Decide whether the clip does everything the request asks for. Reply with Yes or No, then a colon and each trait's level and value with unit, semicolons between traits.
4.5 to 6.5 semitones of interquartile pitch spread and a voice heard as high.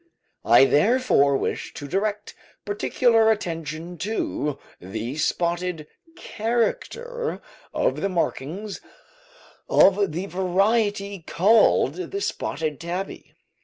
Yes: average, 5.2 semitones; high, 195 Hz